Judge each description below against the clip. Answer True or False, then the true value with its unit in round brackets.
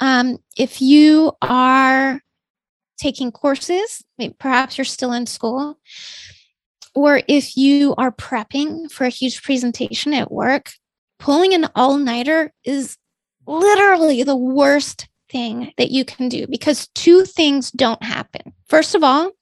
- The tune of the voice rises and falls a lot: False (2.8 semitones)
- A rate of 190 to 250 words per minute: False (135 wpm)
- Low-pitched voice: False (270 Hz)